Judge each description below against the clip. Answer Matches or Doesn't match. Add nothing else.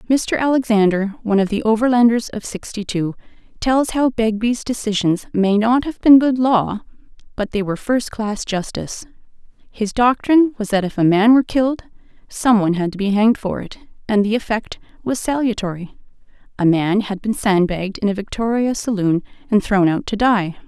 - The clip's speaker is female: Matches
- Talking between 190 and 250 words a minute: Doesn't match